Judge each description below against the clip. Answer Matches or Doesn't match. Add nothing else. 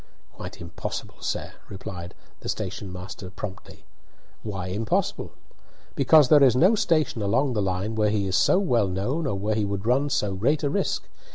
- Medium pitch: Doesn't match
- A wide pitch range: Matches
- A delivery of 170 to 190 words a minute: Matches